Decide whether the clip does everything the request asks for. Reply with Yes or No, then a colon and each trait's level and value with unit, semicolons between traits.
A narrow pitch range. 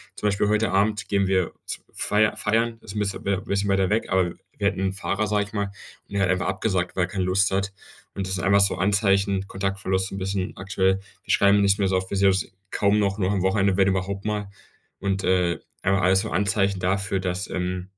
Yes: narrow, 1.0 semitones